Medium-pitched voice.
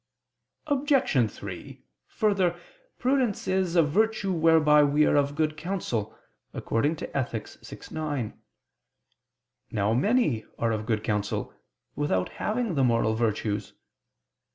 Yes: medium, 150 Hz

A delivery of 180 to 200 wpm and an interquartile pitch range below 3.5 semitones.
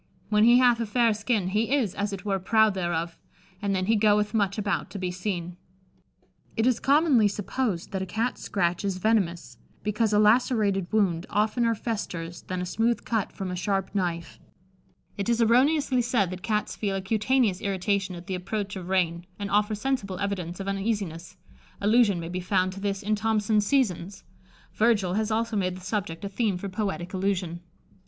Yes: average, 185 wpm; average, 3.1 semitones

